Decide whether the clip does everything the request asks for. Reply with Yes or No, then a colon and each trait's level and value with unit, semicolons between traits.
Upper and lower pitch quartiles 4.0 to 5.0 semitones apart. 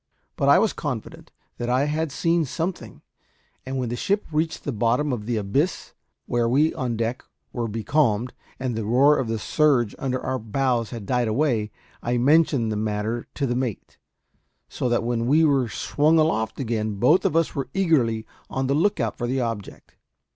Yes: average, 4.3 semitones